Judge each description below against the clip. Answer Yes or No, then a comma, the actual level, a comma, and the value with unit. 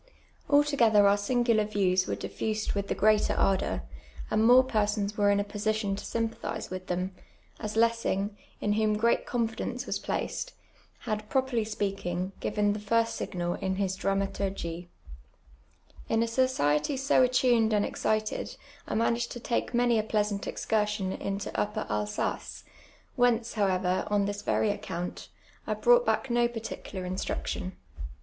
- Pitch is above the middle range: Yes, high, 210 Hz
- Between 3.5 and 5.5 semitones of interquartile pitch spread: No, average, 2.7 semitones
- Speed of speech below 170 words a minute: Yes, average, 145 wpm